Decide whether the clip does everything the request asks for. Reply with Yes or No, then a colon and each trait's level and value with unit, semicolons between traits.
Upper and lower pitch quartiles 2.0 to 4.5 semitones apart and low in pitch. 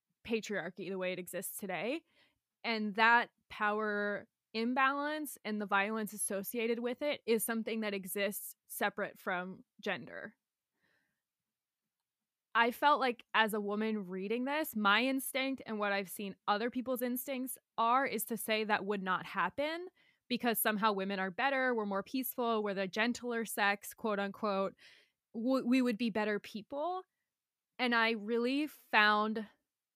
No: average, 3.3 semitones; high, 220 Hz